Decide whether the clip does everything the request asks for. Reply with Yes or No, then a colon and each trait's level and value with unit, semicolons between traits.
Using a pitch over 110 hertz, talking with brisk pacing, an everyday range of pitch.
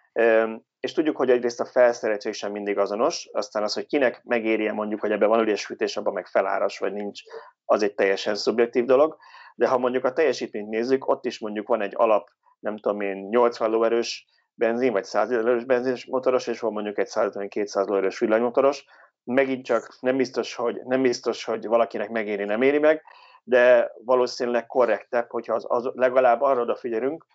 Yes: low, 120 Hz; fast, 180 wpm; average, 3.4 semitones